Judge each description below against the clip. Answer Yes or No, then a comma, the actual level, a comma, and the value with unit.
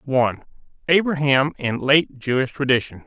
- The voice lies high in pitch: No, low, 135 Hz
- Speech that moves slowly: Yes, slow, 115 wpm